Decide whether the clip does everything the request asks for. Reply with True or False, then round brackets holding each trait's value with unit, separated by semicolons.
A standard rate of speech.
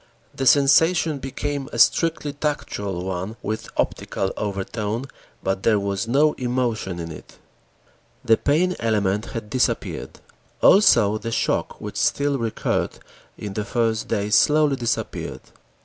False (130 wpm)